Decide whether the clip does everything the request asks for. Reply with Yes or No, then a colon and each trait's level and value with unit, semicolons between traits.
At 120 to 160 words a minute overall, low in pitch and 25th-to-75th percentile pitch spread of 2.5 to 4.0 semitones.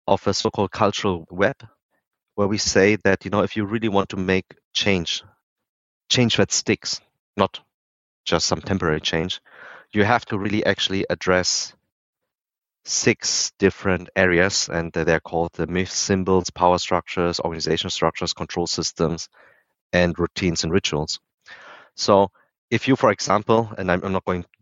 Yes: average, 150 wpm; very low, 95 Hz; average, 2.9 semitones